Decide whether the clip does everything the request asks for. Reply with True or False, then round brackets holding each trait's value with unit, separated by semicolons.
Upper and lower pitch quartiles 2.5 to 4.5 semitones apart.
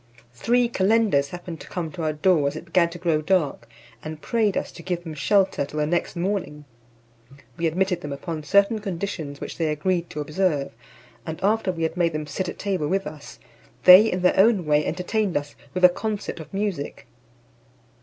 True (4.0 semitones)